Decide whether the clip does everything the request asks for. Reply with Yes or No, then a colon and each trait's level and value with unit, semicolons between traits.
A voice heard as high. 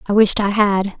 Yes: high, 200 Hz